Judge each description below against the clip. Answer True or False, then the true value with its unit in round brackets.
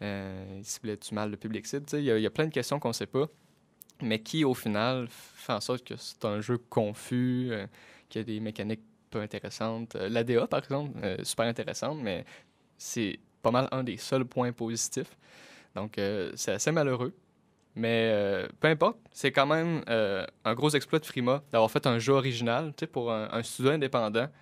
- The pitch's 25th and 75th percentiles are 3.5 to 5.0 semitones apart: True (3.9 semitones)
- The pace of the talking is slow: False (205 wpm)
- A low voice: True (120 Hz)